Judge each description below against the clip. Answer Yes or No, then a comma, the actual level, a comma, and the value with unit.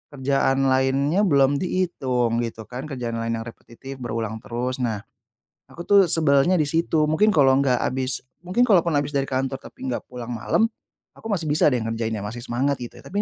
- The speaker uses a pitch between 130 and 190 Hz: Yes, low, 135 Hz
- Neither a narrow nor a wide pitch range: Yes, average, 4.2 semitones